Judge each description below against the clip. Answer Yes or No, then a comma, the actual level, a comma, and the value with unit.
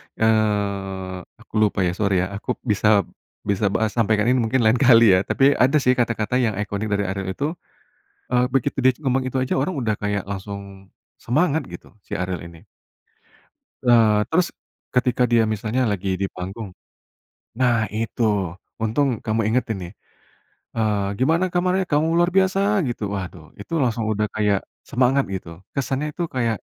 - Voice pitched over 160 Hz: No, low, 110 Hz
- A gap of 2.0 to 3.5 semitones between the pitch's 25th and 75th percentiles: No, average, 4.3 semitones